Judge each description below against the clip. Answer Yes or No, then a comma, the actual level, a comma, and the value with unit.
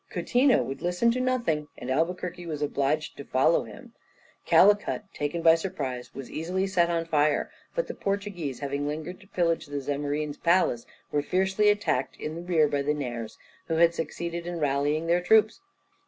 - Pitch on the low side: No, medium, 165 Hz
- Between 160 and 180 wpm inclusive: Yes, average, 170 wpm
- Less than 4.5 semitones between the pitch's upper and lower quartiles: Yes, average, 3.9 semitones